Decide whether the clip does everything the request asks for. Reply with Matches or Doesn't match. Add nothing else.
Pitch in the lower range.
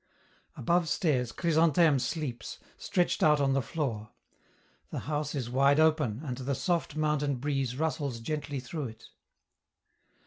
Doesn't match